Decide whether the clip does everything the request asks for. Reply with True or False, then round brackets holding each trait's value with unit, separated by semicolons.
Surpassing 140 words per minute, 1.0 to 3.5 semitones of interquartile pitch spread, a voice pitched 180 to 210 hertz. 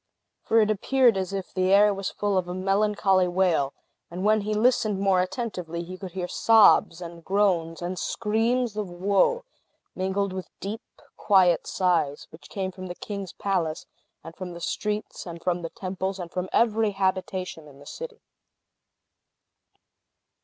True (160 wpm; 2.7 semitones; 190 Hz)